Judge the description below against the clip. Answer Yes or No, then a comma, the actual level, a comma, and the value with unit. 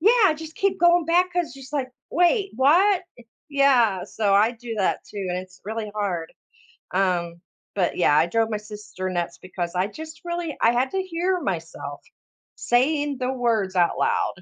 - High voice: Yes, high, 235 Hz